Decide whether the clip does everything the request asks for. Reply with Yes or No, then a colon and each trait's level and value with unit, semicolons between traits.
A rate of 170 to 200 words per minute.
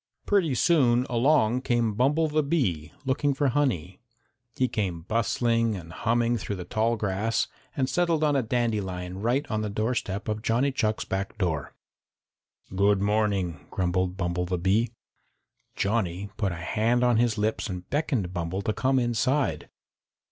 No: average, 155 wpm